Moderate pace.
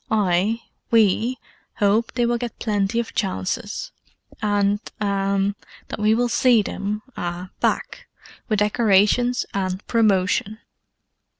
No: slow, 85 wpm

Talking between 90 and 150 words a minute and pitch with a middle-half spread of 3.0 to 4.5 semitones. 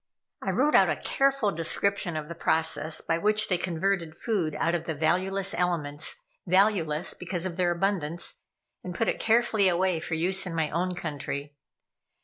No: average, 170 wpm; average, 3.3 semitones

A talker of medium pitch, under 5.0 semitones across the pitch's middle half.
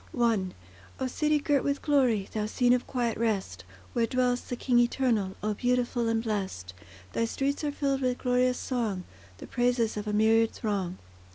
No: high, 240 Hz; average, 3.0 semitones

